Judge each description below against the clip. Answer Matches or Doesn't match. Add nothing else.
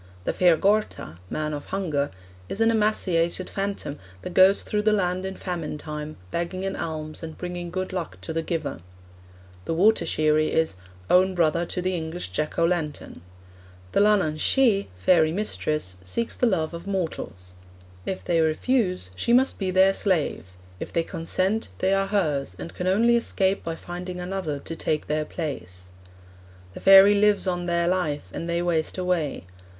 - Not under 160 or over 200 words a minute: Matches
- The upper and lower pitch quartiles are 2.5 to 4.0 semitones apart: Matches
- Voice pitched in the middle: Matches